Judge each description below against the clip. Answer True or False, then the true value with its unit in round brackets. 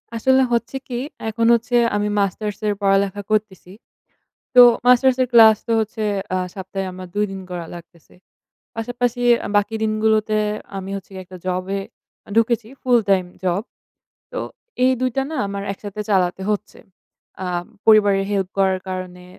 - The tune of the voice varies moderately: True (3.1 semitones)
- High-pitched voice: True (205 Hz)